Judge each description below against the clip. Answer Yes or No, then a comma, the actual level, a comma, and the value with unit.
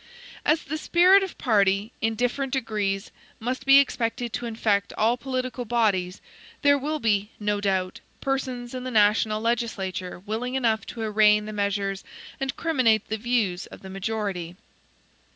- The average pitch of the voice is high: Yes, high, 225 Hz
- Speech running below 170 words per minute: Yes, average, 150 wpm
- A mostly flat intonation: No, average, 3.9 semitones